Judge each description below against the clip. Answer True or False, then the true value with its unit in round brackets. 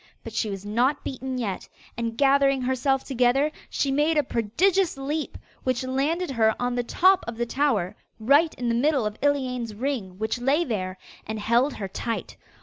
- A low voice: False (255 Hz)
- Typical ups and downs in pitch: True (3.7 semitones)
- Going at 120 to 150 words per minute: False (180 wpm)